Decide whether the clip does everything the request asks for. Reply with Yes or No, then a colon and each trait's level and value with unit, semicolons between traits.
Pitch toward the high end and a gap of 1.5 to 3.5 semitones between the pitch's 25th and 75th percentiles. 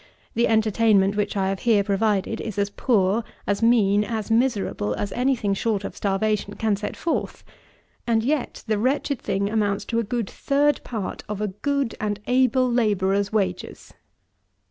Yes: high, 215 Hz; average, 2.9 semitones